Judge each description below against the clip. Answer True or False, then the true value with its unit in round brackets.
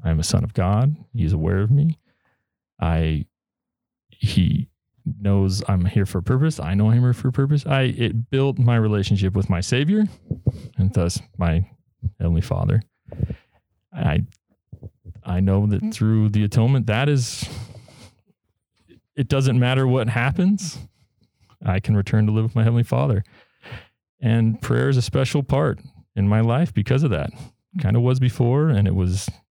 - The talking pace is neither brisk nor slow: True (165 wpm)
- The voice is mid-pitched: False (115 Hz)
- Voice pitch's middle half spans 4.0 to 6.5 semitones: True (4.8 semitones)